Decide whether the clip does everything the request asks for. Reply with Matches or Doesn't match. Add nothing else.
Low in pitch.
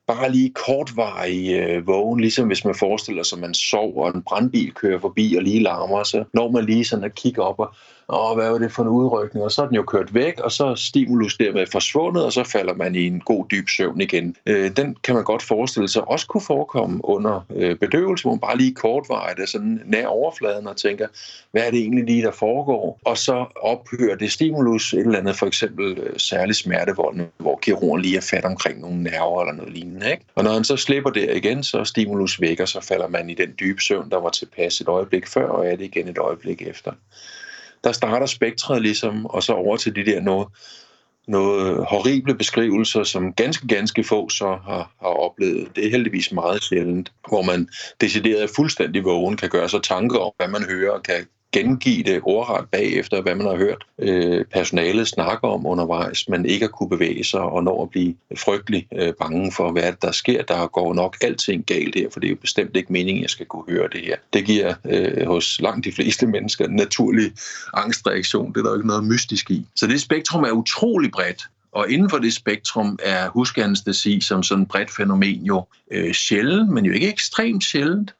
Matches